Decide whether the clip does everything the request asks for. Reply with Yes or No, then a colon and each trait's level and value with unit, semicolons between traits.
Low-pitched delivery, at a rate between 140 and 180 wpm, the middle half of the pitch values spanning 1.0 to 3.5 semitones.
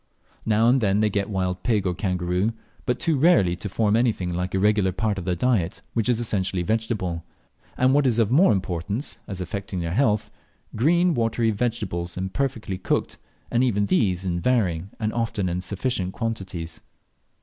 No: low, 105 Hz; average, 175 wpm; average, 4.2 semitones